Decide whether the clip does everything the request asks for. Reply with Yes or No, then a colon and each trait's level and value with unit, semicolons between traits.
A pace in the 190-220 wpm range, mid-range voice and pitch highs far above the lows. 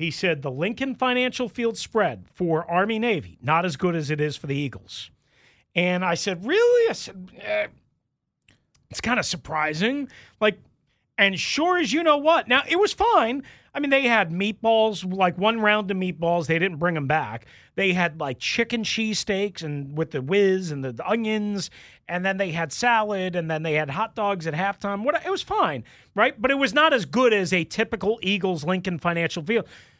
No: average, 200 wpm; high, 195 Hz; wide, 5.7 semitones